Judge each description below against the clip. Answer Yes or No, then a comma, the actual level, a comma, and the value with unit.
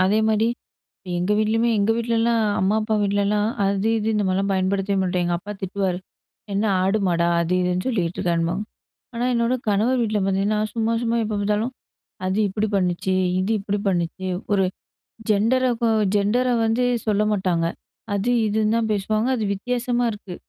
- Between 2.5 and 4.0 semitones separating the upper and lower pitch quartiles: Yes, average, 2.9 semitones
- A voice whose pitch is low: No, high, 205 Hz